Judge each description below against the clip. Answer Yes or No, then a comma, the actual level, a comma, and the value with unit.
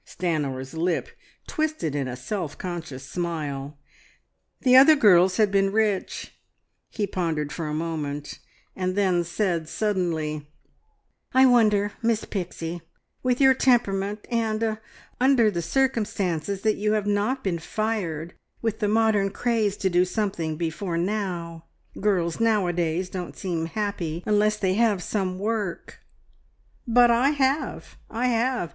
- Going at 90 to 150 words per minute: Yes, average, 140 wpm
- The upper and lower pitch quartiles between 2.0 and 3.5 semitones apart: No, average, 4.6 semitones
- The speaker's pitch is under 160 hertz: No, high, 195 Hz